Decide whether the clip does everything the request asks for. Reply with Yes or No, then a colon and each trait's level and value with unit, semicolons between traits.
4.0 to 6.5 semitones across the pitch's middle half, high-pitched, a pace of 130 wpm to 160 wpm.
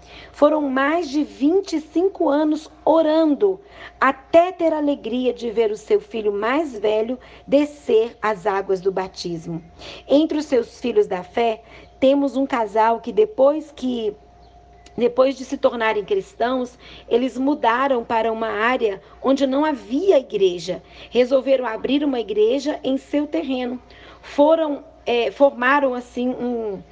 Yes: average, 4.6 semitones; very high, 260 Hz; average, 135 wpm